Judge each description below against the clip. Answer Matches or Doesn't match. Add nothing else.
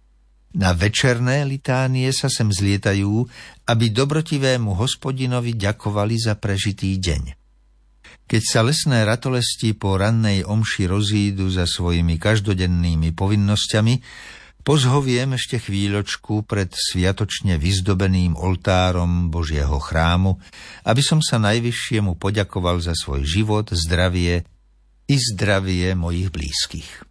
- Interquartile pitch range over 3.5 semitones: Matches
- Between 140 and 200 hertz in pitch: Doesn't match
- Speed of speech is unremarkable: Doesn't match